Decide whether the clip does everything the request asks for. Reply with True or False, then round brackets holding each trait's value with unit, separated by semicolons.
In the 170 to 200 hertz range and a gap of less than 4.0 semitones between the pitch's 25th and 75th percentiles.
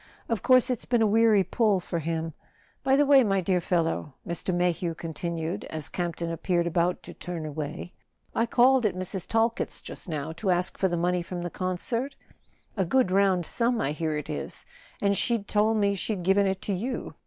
False (185 Hz; 4.5 semitones)